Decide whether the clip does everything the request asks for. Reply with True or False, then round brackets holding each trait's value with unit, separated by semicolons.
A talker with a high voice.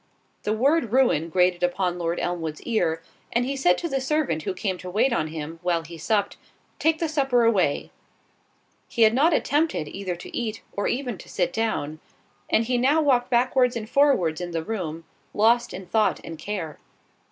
True (210 Hz)